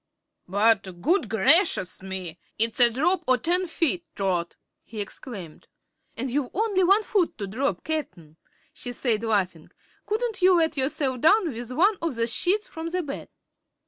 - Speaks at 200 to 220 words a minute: No, average, 160 wpm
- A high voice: Yes, very high, 260 Hz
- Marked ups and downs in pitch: Yes, wide, 8.8 semitones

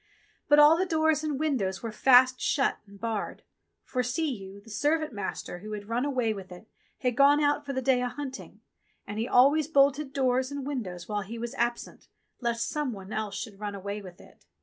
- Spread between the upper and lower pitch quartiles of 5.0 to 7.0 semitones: Yes, average, 5.3 semitones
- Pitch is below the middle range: No, very high, 250 Hz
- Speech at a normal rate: No, fast, 210 wpm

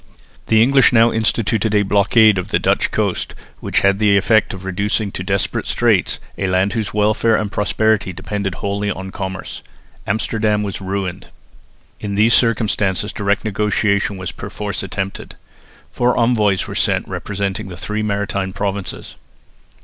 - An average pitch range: No, narrow, 1.8 semitones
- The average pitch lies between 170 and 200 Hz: No, low, 100 Hz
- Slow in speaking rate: No, average, 150 wpm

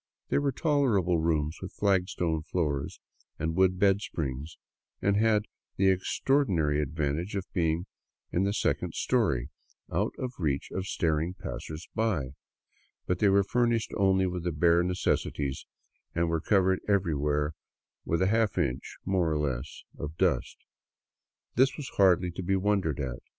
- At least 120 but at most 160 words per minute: Yes, average, 150 wpm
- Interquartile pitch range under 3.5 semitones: No, average, 4.3 semitones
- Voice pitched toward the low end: Yes, very low, 90 Hz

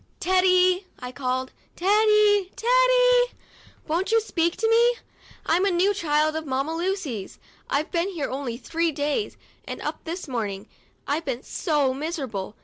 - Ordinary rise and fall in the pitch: No, wide, 6.3 semitones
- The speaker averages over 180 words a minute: No, average, 150 wpm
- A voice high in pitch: Yes, very high, 335 Hz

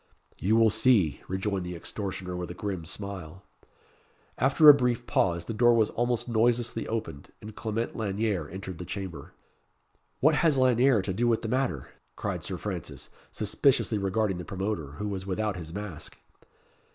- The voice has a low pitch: Yes, low, 105 Hz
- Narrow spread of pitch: No, average, 4.2 semitones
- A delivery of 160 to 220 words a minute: Yes, average, 165 wpm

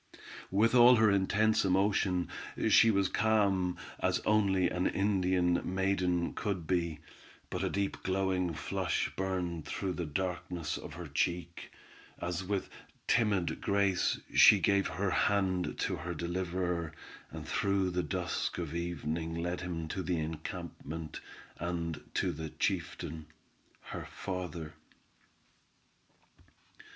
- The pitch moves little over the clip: Yes, narrow, 2.2 semitones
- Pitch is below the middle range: Yes, very low, 90 Hz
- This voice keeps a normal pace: No, slow, 120 wpm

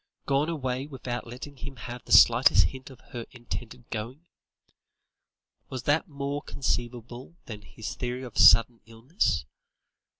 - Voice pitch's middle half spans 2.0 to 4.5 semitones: Yes, average, 2.7 semitones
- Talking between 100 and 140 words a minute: Yes, slow, 135 wpm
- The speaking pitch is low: Yes, low, 125 Hz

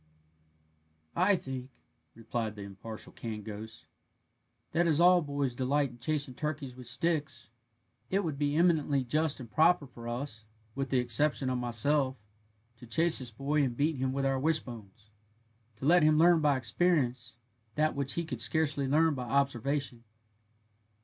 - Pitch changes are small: No, average, 4.1 semitones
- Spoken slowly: No, average, 155 wpm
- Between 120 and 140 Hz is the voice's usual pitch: Yes, low, 135 Hz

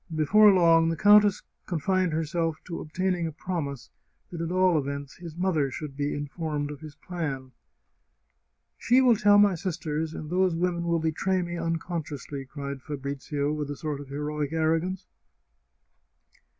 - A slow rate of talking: No, average, 165 wpm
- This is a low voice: No, medium, 160 Hz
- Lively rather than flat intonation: No, average, 3.6 semitones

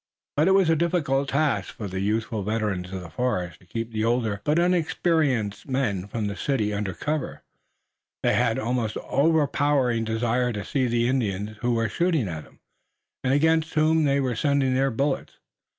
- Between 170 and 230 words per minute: Yes, average, 180 wpm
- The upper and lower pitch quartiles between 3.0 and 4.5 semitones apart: No, wide, 5.4 semitones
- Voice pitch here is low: Yes, low, 125 Hz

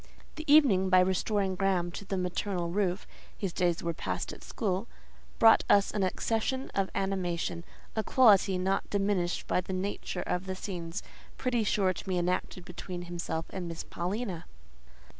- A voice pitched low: No, high, 190 Hz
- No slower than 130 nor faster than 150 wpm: No, average, 160 wpm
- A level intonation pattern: Yes, narrow, 2.3 semitones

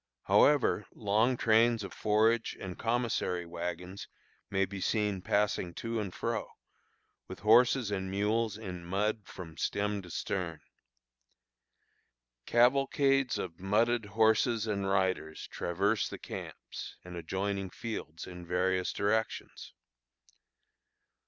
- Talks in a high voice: No, low, 100 Hz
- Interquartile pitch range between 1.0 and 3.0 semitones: No, average, 3.4 semitones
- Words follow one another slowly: Yes, slow, 115 wpm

